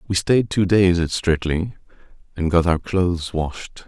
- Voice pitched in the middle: No, very low, 90 Hz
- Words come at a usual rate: Yes, average, 170 wpm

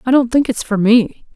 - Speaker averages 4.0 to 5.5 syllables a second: Yes, 5.1 syllables/s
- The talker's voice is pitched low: No, high, 235 Hz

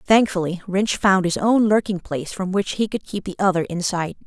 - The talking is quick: Yes, fast, 225 wpm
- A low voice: No, high, 190 Hz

